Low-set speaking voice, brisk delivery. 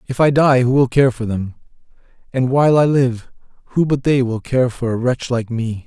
Yes: low, 125 Hz; fast, 225 wpm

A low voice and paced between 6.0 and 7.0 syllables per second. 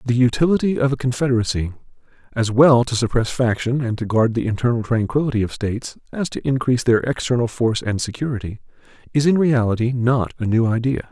Yes: low, 120 Hz; 6.1 syllables/s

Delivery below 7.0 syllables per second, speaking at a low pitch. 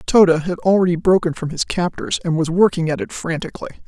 No: 5.9 syllables/s; medium, 175 Hz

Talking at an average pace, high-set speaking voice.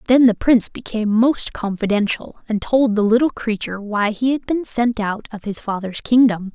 Yes: average, 190 wpm; high, 225 Hz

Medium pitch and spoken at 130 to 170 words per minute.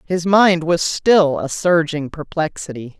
Yes: medium, 165 Hz; average, 140 wpm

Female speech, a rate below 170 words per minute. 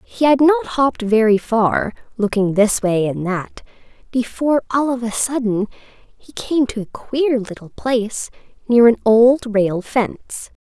Yes: female; average, 160 wpm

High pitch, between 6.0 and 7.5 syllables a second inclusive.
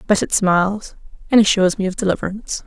Yes: high, 195 Hz; 6.9 syllables/s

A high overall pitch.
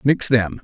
No: low, 120 Hz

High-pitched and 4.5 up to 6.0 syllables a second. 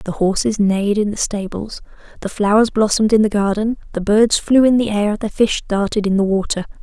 Yes: high, 210 Hz; 5.5 syllables/s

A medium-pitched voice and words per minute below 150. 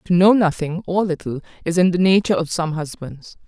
No: medium, 170 Hz; fast, 205 wpm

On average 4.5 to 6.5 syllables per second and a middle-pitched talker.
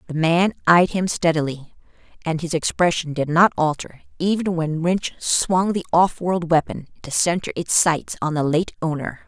Yes: 4.6 syllables/s; medium, 165 Hz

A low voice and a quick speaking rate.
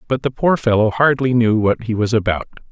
Yes: low, 115 Hz; fast, 220 wpm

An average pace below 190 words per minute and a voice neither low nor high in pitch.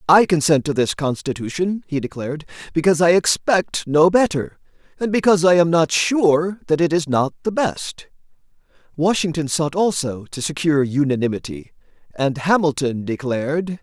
Yes: average, 145 wpm; medium, 160 Hz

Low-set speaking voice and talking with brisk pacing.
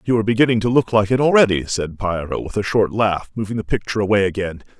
Yes: low, 105 Hz; fast, 240 wpm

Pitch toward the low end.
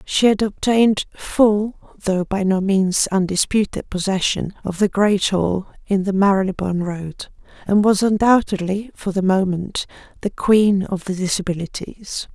No: high, 195 Hz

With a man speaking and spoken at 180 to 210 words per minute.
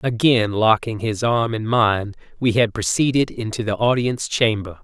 No: male; average, 160 wpm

